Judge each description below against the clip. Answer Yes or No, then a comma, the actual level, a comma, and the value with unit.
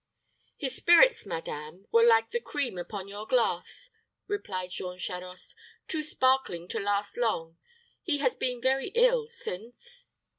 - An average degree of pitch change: No, wide, 8.7 semitones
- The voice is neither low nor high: No, high, 230 Hz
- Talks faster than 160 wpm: No, average, 140 wpm